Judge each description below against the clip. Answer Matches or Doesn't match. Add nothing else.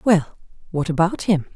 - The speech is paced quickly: Doesn't match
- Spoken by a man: Doesn't match